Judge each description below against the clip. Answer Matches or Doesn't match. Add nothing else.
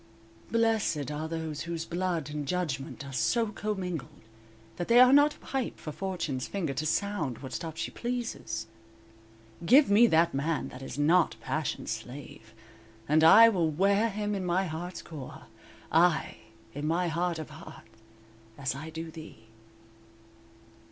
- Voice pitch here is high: Doesn't match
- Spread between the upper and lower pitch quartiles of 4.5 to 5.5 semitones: Matches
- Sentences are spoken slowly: Doesn't match